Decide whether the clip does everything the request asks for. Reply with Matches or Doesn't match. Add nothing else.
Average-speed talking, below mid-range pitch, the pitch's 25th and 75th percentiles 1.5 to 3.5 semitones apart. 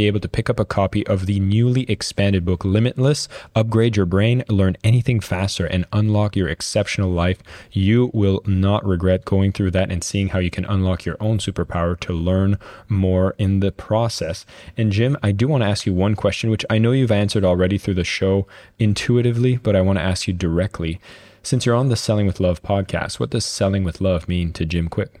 Doesn't match